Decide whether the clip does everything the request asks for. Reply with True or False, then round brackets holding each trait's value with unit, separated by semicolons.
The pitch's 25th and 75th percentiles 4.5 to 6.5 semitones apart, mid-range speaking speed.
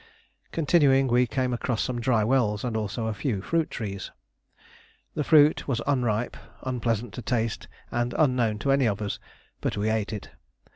False (3.5 semitones; 165 wpm)